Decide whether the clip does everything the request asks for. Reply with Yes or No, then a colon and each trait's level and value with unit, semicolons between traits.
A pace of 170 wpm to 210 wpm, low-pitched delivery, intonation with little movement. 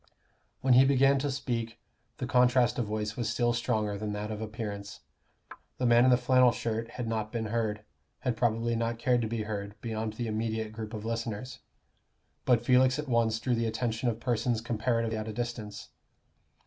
Yes: average, 185 wpm; low, 115 Hz; narrow, 2.1 semitones